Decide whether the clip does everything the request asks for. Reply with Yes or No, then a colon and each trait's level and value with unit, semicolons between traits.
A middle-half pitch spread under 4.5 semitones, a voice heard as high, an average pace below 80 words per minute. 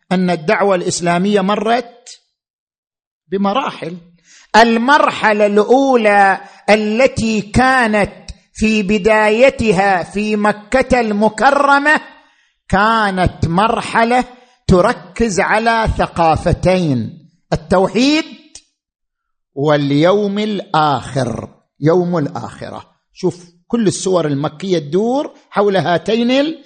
No: average, 5.2 semitones; high, 205 Hz; average, 70 wpm